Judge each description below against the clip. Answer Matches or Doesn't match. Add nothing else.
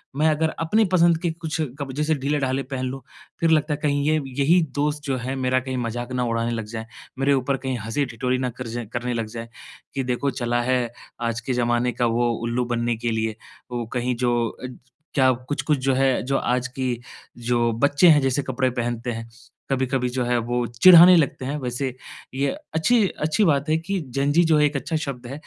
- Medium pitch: Doesn't match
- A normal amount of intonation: Matches